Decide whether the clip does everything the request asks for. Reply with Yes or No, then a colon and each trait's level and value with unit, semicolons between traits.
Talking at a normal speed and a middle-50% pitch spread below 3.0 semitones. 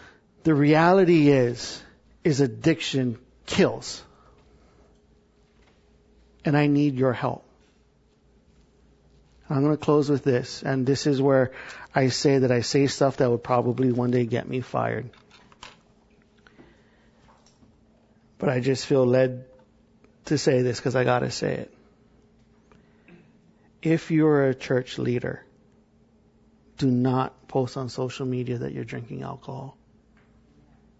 No: slow, 125 wpm; narrow, 2.5 semitones